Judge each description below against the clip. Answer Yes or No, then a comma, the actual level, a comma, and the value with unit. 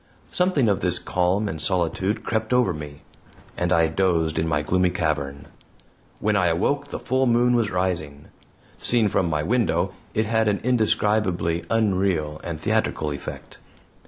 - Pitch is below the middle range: Yes, very low, 95 Hz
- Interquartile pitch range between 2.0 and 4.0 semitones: No, average, 5.3 semitones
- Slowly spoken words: No, average, 155 wpm